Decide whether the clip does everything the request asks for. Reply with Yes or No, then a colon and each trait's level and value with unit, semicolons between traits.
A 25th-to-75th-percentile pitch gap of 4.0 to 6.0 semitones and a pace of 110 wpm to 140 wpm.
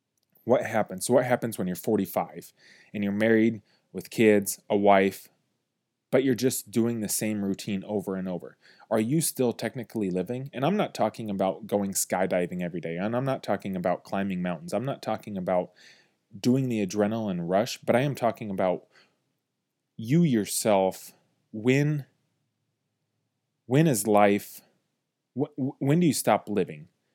No: average, 5.1 semitones; average, 155 wpm